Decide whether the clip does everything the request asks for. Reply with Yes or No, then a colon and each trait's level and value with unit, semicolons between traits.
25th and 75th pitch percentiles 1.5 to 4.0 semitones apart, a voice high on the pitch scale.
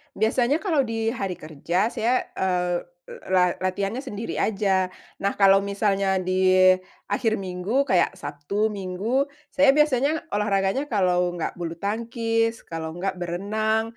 Yes: average, 3.7 semitones; high, 200 Hz